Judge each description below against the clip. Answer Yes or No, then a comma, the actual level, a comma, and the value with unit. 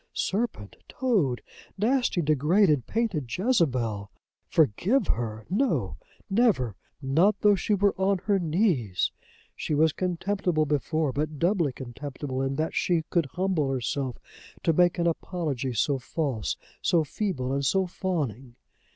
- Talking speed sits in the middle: No, slow, 130 wpm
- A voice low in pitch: No, medium, 155 Hz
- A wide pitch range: Yes, wide, 6.3 semitones